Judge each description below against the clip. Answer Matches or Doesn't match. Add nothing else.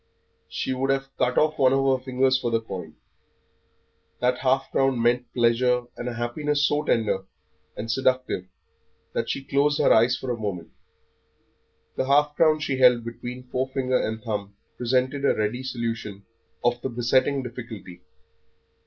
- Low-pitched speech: Matches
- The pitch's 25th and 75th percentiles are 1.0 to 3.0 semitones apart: Matches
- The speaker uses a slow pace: Doesn't match